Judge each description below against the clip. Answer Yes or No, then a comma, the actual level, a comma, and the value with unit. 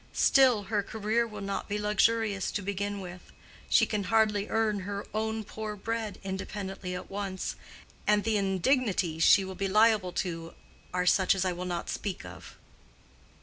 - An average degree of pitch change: No, narrow, 2.3 semitones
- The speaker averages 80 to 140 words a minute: No, average, 165 wpm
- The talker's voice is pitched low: No, high, 200 Hz